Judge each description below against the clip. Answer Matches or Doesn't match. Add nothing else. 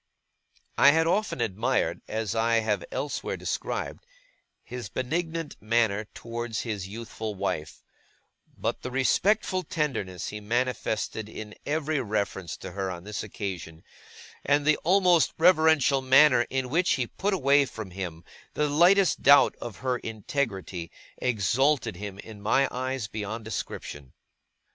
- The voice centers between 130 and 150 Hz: Doesn't match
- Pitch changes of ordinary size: Doesn't match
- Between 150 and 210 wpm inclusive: Doesn't match